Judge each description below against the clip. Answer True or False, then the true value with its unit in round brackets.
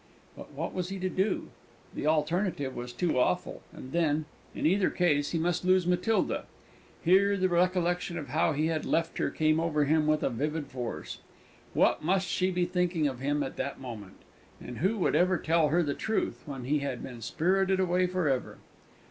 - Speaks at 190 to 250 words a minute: True (195 wpm)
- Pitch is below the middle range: False (165 Hz)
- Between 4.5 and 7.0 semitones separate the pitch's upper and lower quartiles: False (3.9 semitones)